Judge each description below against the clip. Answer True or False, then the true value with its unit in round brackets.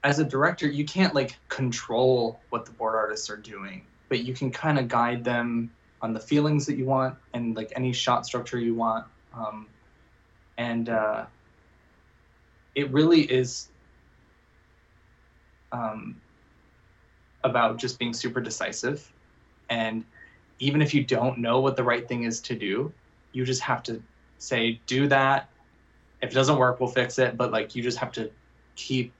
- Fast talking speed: False (160 wpm)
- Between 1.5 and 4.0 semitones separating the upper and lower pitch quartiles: True (2.8 semitones)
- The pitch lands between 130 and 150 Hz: False (120 Hz)